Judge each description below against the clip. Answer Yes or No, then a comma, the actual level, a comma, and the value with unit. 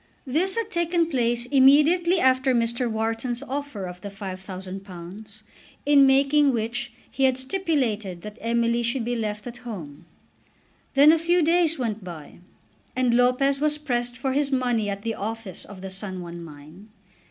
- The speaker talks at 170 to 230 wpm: No, average, 160 wpm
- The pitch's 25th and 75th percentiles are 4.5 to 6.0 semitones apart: Yes, average, 5.1 semitones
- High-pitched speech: Yes, high, 240 Hz